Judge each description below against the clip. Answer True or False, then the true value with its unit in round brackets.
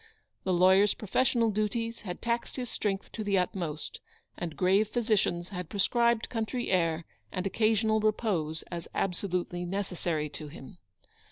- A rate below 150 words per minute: True (140 wpm)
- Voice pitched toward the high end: True (195 Hz)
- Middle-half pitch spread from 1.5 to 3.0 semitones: False (3.8 semitones)